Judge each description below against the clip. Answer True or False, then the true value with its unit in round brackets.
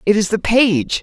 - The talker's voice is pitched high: True (220 Hz)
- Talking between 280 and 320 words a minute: False (235 wpm)